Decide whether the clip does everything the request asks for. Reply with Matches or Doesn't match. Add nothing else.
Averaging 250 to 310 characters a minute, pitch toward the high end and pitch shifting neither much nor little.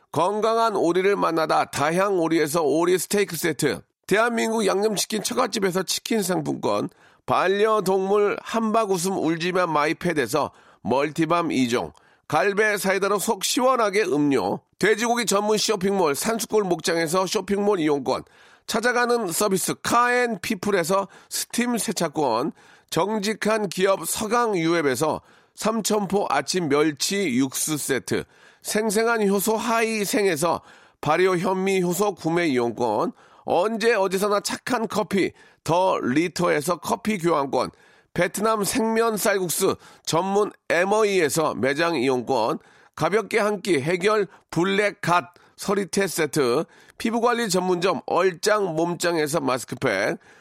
Matches